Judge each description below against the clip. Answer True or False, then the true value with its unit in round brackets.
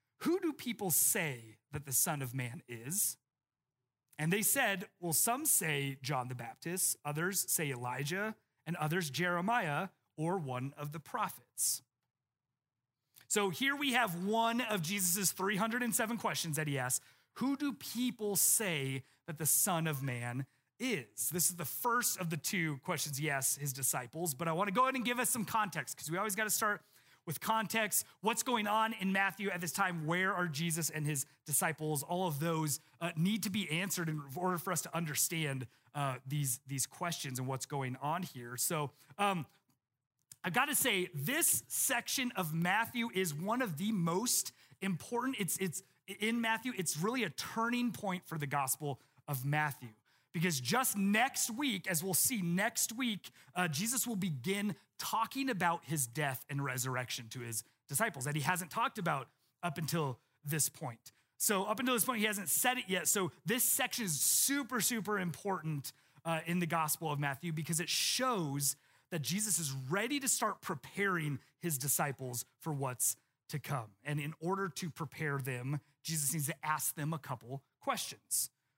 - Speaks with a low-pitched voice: False (165 Hz)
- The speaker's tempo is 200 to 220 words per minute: False (175 wpm)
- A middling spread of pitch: False (6.4 semitones)